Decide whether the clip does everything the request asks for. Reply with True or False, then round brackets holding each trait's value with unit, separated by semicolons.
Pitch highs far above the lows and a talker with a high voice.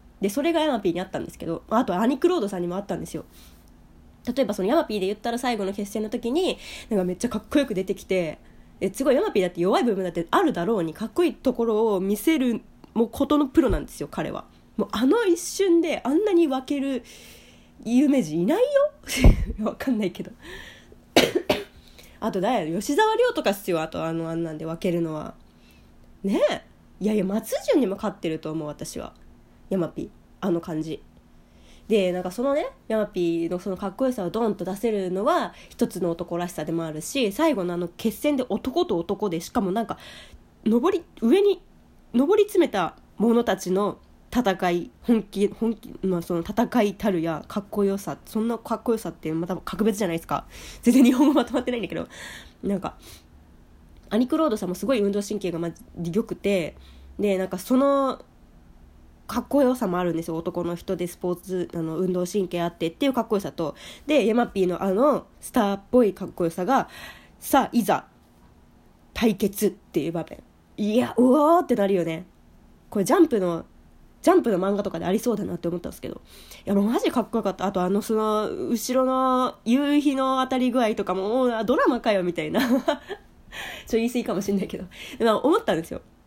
True (6.1 semitones; 210 Hz)